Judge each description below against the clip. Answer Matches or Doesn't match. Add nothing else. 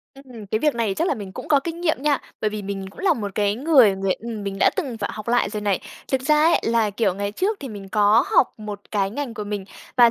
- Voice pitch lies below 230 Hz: Matches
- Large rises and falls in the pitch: Doesn't match